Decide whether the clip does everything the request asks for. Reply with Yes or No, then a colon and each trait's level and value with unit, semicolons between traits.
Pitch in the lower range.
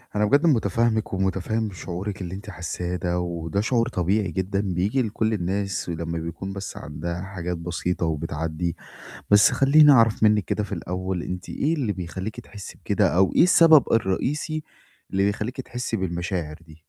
Yes: very low, 95 Hz